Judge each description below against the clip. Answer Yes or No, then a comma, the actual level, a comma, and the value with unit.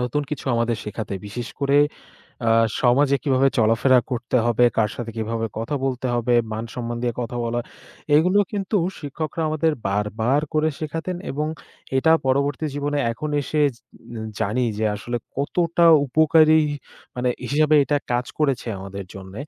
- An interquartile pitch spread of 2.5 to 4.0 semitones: No, average, 4.6 semitones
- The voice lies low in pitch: Yes, low, 130 Hz